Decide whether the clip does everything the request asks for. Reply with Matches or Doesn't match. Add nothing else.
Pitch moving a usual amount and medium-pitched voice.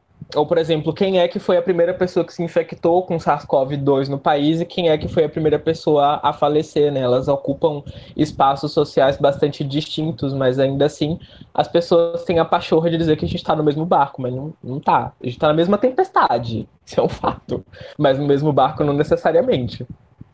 Matches